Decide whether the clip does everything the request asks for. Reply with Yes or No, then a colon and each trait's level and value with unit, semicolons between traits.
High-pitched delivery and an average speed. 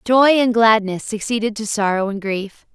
Yes: high, 215 Hz; average, 175 wpm